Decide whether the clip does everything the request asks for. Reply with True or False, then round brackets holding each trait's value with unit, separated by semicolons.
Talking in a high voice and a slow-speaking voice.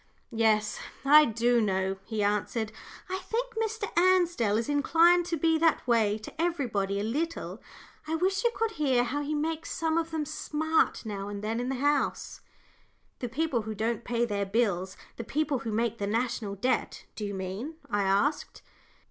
False (245 Hz; 180 wpm)